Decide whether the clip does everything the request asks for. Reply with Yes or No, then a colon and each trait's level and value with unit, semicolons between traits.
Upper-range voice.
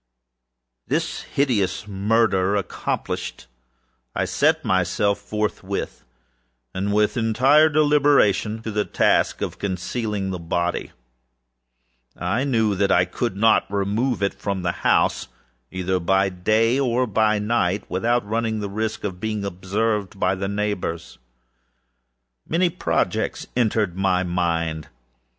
No: low, 105 Hz